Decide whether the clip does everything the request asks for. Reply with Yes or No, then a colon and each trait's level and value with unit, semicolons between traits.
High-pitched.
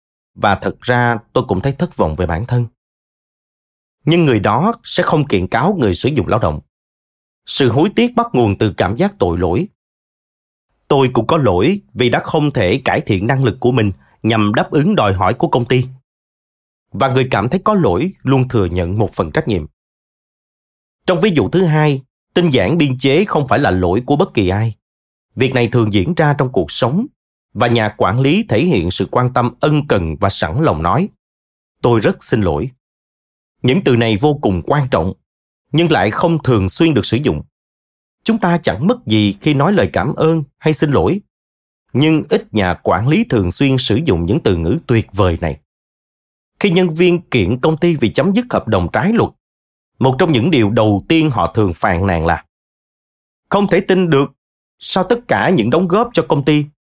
No: low, 120 Hz